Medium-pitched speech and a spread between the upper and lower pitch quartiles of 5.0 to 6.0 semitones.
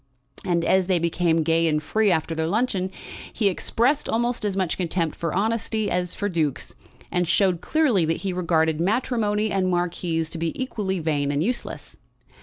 No: medium, 180 Hz; average, 4.2 semitones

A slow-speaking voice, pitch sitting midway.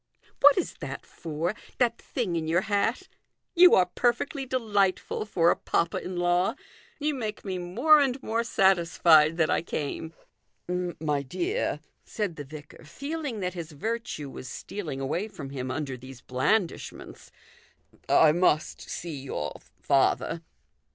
No: average, 150 wpm; medium, 175 Hz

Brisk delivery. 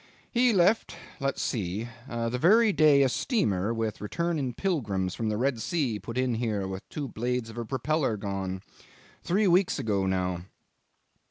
No: average, 160 wpm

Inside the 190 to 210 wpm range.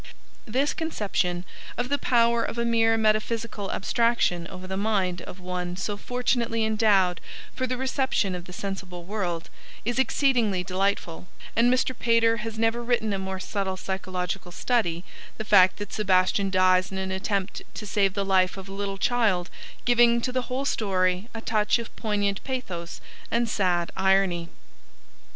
No: average, 160 wpm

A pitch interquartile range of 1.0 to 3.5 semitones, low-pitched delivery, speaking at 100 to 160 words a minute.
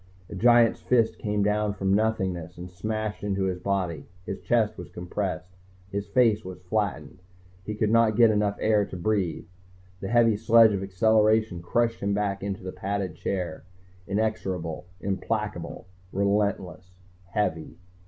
Yes: average, 2.8 semitones; low, 100 Hz; average, 150 wpm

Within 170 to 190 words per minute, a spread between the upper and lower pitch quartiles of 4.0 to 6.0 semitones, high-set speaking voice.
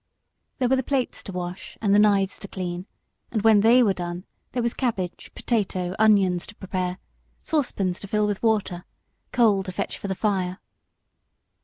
No: average, 175 wpm; average, 3.4 semitones; high, 200 Hz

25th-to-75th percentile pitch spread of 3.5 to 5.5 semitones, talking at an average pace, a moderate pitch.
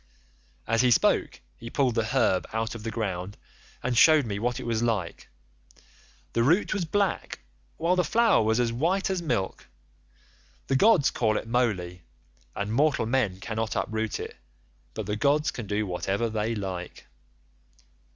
No: average, 4.6 semitones; average, 160 wpm; low, 115 Hz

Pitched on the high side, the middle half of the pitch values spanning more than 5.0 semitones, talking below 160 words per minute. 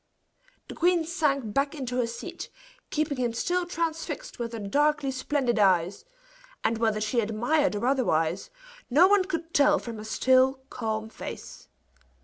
Yes: very high, 260 Hz; wide, 5.6 semitones; average, 150 wpm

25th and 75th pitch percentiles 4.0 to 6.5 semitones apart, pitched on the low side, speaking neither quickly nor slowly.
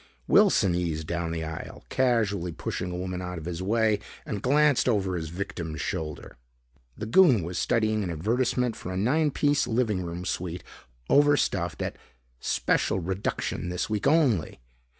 Yes: average, 5.1 semitones; very low, 95 Hz; average, 155 wpm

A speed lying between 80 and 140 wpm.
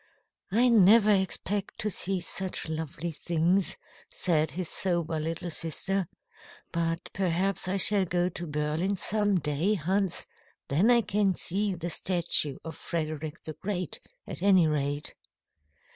Yes: slow, 135 wpm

